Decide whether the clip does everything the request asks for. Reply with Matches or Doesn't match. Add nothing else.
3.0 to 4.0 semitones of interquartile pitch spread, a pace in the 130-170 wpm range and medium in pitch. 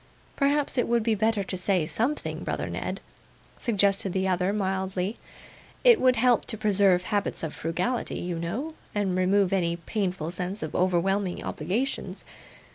Doesn't match